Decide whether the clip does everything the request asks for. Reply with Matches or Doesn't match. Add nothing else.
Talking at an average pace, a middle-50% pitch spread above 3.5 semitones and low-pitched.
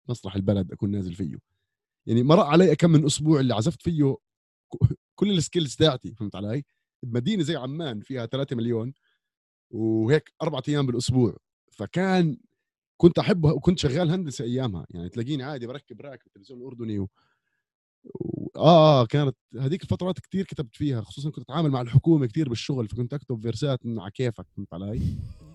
Doesn't match